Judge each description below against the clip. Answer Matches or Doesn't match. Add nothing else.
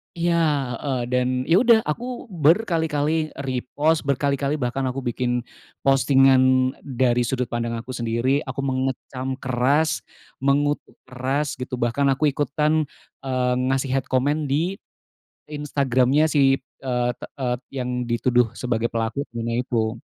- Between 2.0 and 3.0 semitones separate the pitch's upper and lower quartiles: Matches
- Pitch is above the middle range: Doesn't match